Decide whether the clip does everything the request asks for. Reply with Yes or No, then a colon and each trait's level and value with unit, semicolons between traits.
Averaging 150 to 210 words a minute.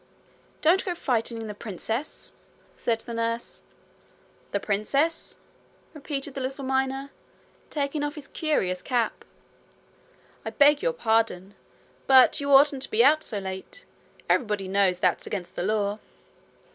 No: slow, 135 wpm